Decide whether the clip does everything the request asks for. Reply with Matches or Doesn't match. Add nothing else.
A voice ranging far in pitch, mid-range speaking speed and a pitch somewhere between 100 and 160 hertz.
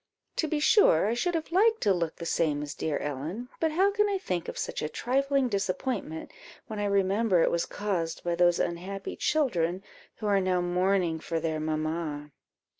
Doesn't match